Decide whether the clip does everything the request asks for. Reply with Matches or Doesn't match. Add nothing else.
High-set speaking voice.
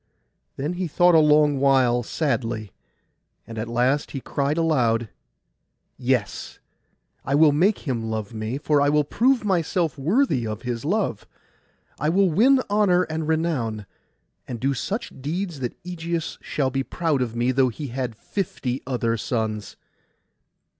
Doesn't match